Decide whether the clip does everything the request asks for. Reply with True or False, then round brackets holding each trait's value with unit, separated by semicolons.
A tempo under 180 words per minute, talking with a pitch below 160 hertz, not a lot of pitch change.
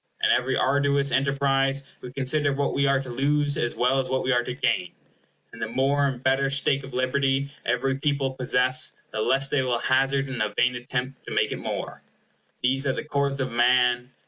False (205 wpm; 135 Hz; 1.6 semitones)